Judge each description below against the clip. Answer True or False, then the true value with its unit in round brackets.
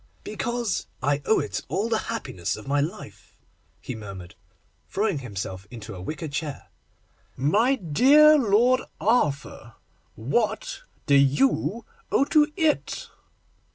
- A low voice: False (175 Hz)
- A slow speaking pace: True (125 wpm)